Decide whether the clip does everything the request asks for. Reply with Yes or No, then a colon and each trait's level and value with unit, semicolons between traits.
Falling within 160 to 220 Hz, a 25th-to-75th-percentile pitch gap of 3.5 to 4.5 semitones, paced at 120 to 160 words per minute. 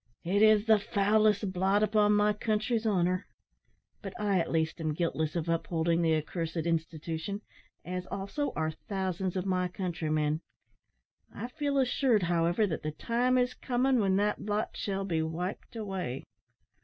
Yes: high, 190 Hz; average, 4.1 semitones; average, 155 wpm